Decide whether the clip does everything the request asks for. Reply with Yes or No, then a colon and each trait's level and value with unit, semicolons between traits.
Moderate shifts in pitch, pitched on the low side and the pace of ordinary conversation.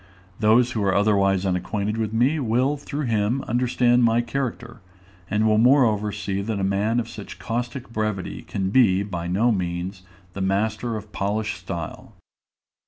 Yes: average, 3.4 semitones; low, 110 Hz; average, 160 wpm